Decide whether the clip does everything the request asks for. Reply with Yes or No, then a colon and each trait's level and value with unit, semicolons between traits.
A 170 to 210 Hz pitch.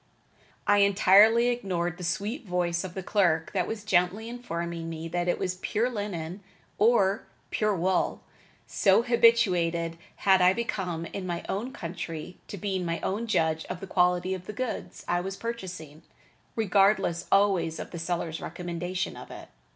Yes: medium, 185 Hz